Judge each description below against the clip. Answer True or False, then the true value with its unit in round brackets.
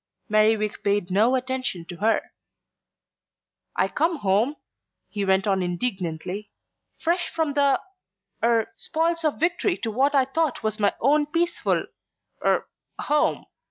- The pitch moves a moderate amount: False (6.8 semitones)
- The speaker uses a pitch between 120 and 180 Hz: False (240 Hz)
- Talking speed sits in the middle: False (130 wpm)